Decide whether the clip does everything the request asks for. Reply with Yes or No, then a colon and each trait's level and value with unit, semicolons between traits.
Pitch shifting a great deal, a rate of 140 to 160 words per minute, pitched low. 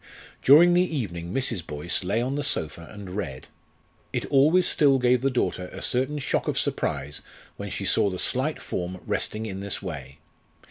No: wide, 7.6 semitones; average, 180 wpm; low, 105 Hz